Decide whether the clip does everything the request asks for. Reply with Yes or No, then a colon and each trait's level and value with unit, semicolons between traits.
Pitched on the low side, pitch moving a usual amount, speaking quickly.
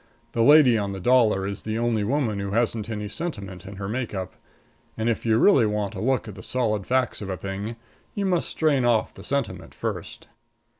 Yes: low, 110 Hz; average, 4.1 semitones; fast, 210 wpm